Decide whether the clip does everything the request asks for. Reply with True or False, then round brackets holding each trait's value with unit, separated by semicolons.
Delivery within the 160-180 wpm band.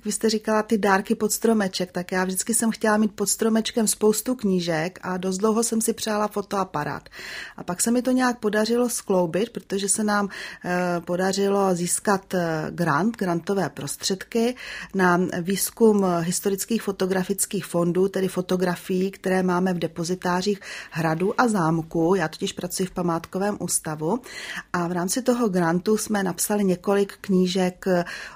False (145 wpm)